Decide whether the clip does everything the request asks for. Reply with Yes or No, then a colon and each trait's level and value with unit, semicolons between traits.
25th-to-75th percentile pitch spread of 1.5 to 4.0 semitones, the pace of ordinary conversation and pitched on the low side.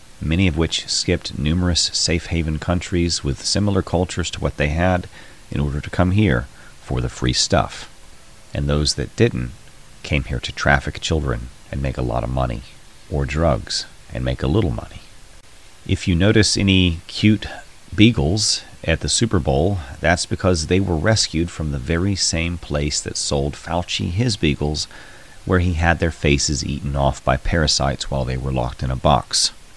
No: average, 5.0 semitones; average, 175 wpm; very low, 85 Hz